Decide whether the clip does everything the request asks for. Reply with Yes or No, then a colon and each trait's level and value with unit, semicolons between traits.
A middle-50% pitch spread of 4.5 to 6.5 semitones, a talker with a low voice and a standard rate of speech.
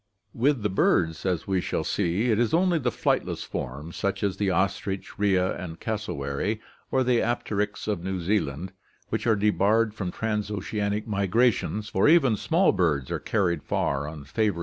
No: average, 3.7 semitones; low, 100 Hz; average, 175 wpm